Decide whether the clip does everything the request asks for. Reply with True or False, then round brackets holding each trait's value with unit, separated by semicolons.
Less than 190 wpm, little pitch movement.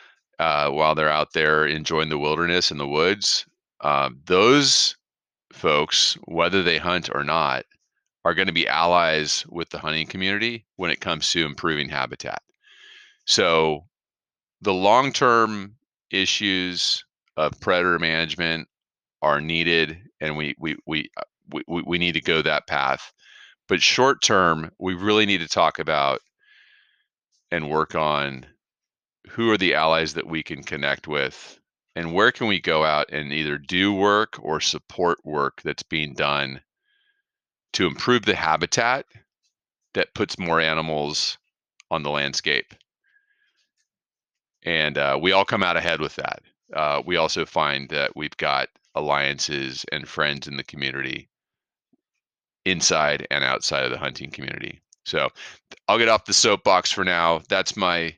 False (145 wpm; 4.5 semitones)